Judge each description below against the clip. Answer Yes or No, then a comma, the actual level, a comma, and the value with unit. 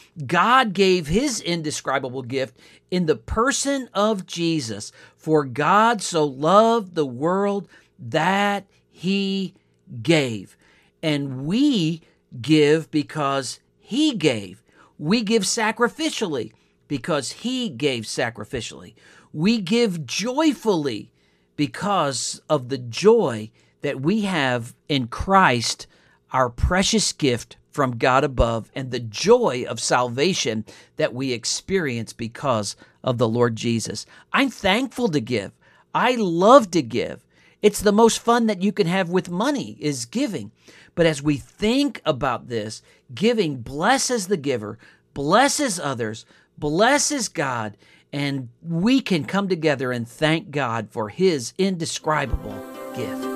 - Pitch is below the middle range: No, medium, 160 Hz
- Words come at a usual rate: No, slow, 125 wpm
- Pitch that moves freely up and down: Yes, wide, 8.2 semitones